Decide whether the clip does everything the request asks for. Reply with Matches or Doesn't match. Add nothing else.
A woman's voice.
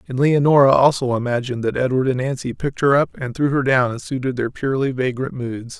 Doesn't match